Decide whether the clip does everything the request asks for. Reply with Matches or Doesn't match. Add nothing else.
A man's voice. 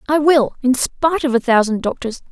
Doesn't match